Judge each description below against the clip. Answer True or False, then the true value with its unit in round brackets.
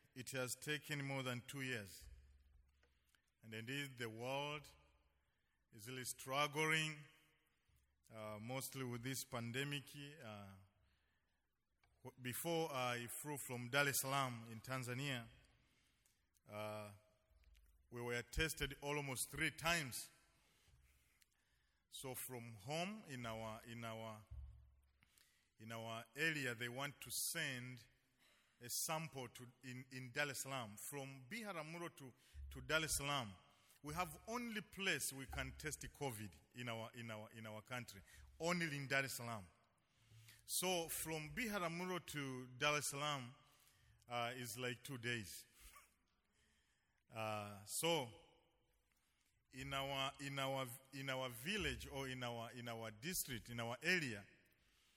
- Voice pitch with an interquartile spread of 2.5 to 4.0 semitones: False (4.6 semitones)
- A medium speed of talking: False (125 wpm)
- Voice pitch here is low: True (125 Hz)